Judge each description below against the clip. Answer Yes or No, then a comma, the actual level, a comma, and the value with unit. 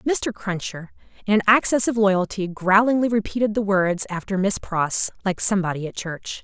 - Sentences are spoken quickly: No, average, 170 wpm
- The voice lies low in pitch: No, high, 200 Hz